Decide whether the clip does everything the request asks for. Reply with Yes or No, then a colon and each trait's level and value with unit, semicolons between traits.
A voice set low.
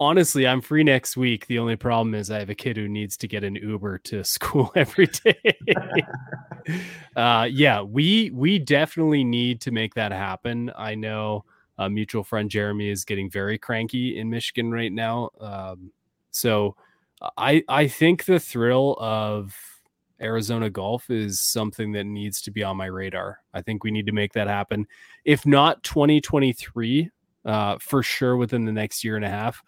Yes: low, 115 Hz